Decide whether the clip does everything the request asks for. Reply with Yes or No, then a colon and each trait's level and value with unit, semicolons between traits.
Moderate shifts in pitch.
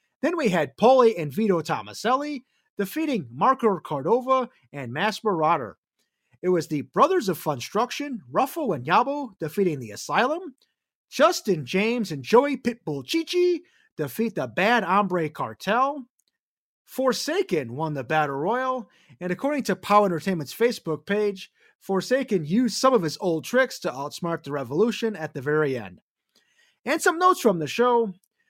No: wide, 8.3 semitones